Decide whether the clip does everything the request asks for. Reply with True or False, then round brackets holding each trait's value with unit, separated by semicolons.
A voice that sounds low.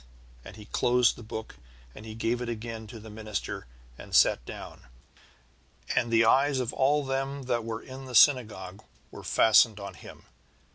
True (115 Hz)